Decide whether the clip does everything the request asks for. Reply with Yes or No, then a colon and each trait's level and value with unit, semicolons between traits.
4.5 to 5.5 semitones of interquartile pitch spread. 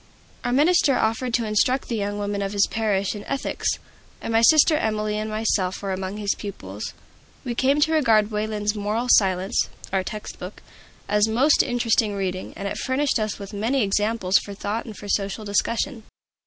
No: average, 2.7 semitones